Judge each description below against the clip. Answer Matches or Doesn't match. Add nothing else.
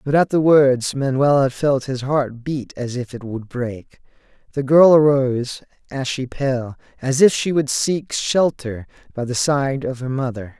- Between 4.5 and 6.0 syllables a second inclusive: Doesn't match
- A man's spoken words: Matches